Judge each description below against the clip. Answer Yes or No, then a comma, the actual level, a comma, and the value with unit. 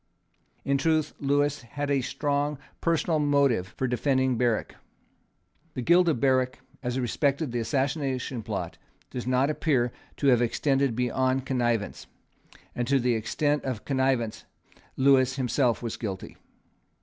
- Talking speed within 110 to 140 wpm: Yes, slow, 135 wpm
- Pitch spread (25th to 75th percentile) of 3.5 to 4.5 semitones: No, average, 2.7 semitones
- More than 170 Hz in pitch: No, low, 130 Hz